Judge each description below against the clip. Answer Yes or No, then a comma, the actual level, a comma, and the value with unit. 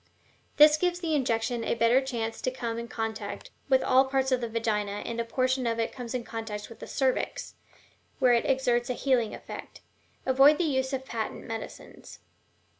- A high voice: Yes, high, 245 Hz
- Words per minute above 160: Yes, average, 190 wpm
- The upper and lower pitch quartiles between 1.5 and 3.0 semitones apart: Yes, narrow, 2.6 semitones